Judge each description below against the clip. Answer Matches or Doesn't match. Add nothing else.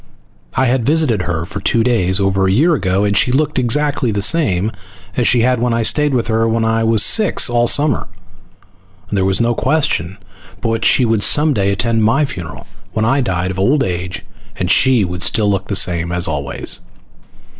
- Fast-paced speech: Matches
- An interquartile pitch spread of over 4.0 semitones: Matches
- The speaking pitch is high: Doesn't match